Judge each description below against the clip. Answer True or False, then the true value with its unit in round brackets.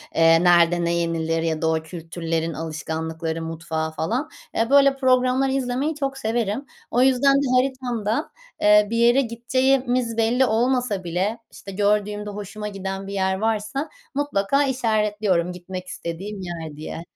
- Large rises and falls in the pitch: True (6.8 semitones)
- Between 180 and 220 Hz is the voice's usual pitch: True (210 Hz)